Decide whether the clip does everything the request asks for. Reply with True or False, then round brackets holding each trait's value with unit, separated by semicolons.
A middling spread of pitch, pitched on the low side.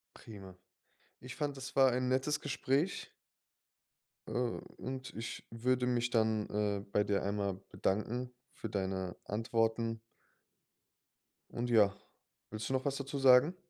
True (3.7 semitones; 120 Hz)